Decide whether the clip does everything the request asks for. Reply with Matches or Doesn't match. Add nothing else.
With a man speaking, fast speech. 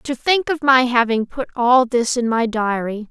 Doesn't match